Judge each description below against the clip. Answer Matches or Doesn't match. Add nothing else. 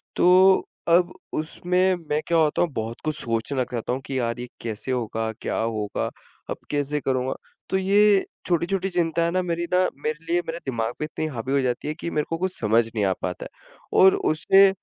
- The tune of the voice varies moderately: Doesn't match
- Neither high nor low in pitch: Matches